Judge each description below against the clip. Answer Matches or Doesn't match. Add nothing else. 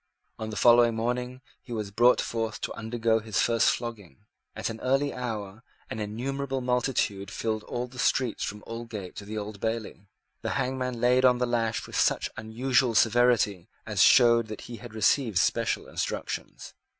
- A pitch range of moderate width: Doesn't match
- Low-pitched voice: Matches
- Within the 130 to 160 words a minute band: Doesn't match